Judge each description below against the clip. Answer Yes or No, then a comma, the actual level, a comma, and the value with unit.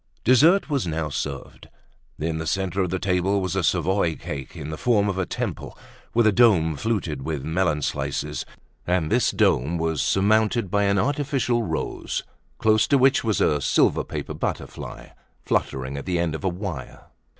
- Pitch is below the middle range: Yes, very low, 95 Hz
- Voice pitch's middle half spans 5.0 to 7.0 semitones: Yes, average, 5.3 semitones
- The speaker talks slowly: No, average, 175 wpm